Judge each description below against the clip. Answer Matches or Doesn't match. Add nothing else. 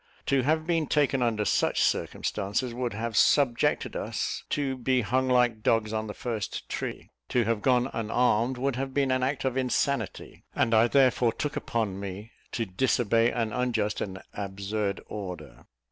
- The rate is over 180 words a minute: Doesn't match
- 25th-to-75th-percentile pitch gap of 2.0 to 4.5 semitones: Matches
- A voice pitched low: Matches